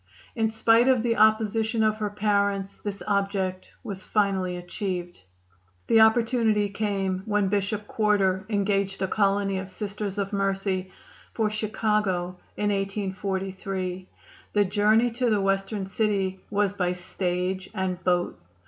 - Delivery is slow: Yes, slow, 130 wpm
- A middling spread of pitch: No, narrow, 2.0 semitones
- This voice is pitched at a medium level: No, high, 200 Hz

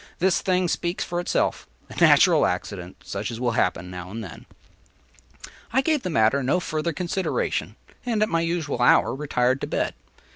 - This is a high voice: No, medium, 150 Hz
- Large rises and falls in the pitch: Yes, wide, 8.2 semitones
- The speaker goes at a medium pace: Yes, average, 175 wpm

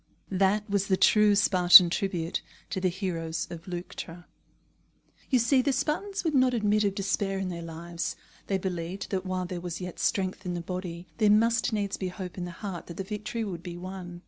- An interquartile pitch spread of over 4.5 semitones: No, average, 2.8 semitones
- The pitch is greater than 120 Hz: Yes, high, 190 Hz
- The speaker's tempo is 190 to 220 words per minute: Yes, average, 200 wpm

